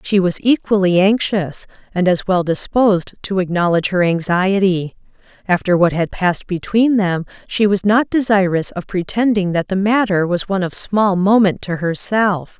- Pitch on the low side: No, high, 190 Hz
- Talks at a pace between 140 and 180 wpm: Yes, average, 160 wpm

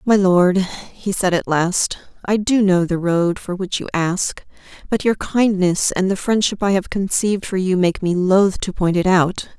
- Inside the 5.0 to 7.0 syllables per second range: No, 4.2 syllables/s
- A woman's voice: Yes, female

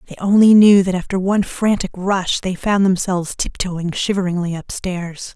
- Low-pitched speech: No, high, 190 Hz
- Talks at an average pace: Yes, average, 155 wpm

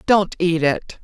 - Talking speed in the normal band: Yes, average, 175 wpm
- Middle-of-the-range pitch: Yes, medium, 175 Hz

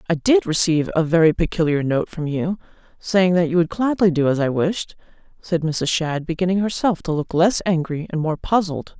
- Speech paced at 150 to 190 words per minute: No, average, 200 wpm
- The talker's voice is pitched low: No, medium, 170 Hz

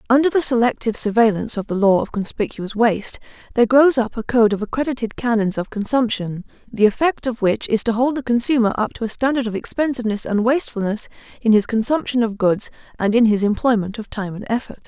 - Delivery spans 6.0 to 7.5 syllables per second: Yes, 6.2 syllables/s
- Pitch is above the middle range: Yes, high, 225 Hz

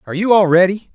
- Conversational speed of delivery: No, fast, 255 wpm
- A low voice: No, high, 190 Hz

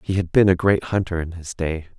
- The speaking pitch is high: No, very low, 90 Hz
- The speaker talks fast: Yes, fast, 270 wpm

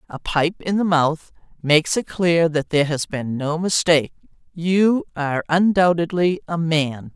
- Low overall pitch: No, medium, 165 Hz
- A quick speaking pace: No, average, 150 wpm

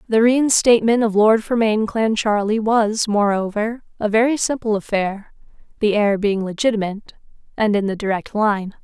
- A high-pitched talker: Yes, high, 215 Hz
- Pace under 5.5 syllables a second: Yes, 4.9 syllables/s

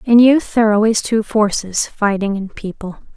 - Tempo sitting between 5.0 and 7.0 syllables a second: Yes, 5.5 syllables/s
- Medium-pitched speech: No, high, 215 Hz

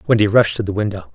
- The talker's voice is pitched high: No, low, 105 Hz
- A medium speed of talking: No, fast, 265 wpm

